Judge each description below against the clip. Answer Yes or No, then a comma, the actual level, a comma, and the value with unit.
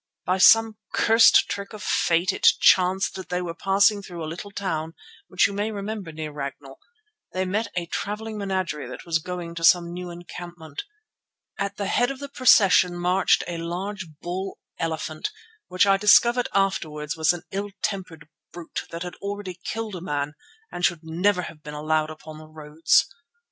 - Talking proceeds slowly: No, average, 180 wpm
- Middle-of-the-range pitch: Yes, medium, 180 Hz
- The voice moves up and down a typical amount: Yes, average, 3.6 semitones